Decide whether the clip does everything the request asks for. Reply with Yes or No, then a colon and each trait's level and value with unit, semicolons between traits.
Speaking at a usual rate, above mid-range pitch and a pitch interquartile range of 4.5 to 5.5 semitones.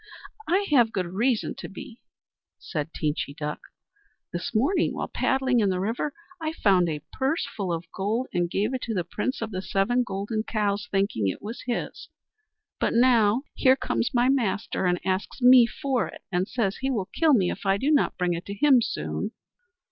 Yes: average, 195 wpm; high, 215 Hz; average, 5.2 semitones